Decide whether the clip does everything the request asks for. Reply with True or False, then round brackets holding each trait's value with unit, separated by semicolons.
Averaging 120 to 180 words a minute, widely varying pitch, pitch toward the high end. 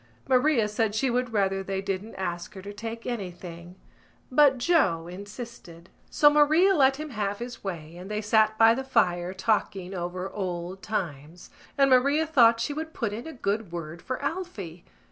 True (175 wpm; 5.7 semitones; 210 Hz)